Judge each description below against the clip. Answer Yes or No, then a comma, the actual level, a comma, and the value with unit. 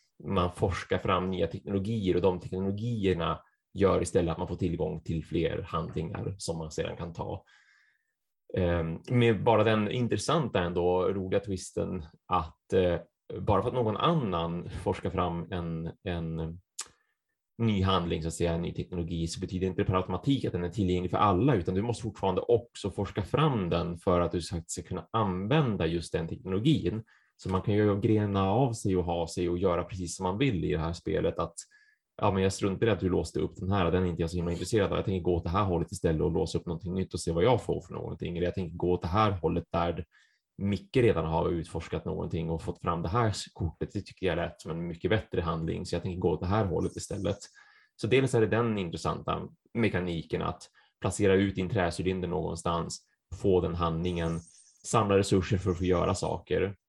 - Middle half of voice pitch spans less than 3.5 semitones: Yes, average, 3.0 semitones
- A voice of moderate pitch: No, very low, 90 Hz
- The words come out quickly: Yes, fast, 210 wpm